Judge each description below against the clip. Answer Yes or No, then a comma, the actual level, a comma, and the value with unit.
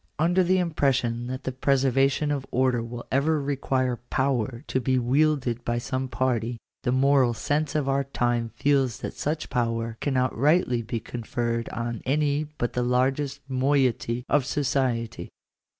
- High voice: No, low, 130 Hz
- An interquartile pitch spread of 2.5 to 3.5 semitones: Yes, average, 2.8 semitones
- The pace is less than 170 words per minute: Yes, average, 155 wpm